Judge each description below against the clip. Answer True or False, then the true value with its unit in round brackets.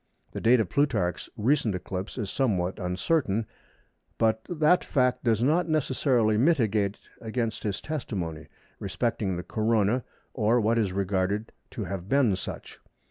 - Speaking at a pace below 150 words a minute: True (135 wpm)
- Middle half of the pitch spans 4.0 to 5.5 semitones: True (4.5 semitones)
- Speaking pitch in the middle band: False (110 Hz)